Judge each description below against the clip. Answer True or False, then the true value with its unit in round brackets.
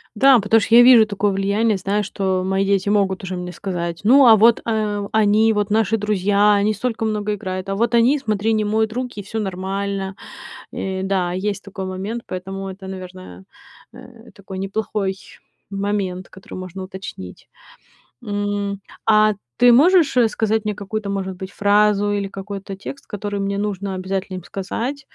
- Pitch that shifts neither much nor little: False (2.1 semitones)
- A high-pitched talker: True (200 Hz)